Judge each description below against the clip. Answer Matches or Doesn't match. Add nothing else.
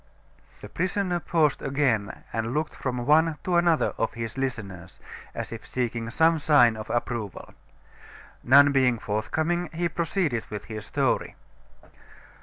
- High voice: Doesn't match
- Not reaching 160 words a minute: Matches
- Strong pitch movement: Matches